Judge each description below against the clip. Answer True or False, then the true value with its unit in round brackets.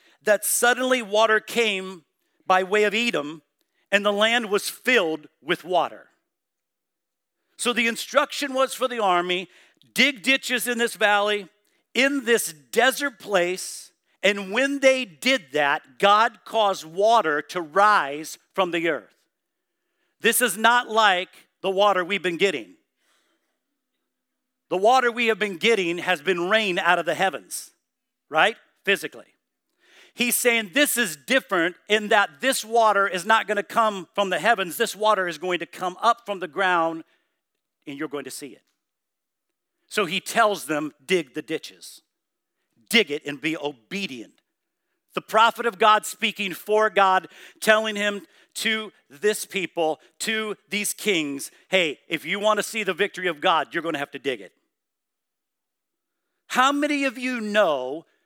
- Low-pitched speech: False (205 Hz)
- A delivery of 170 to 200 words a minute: False (150 wpm)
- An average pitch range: True (4.6 semitones)